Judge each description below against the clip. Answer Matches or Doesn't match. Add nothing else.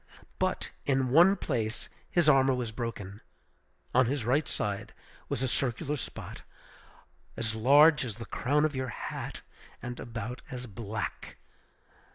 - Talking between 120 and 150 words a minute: Matches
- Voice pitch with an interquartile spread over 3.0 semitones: Matches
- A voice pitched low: Matches